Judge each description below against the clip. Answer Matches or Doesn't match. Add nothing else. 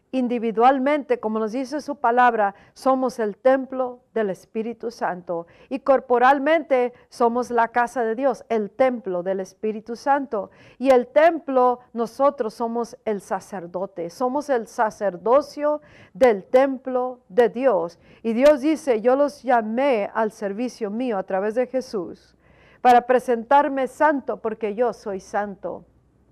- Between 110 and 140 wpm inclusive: Matches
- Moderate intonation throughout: Matches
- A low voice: Doesn't match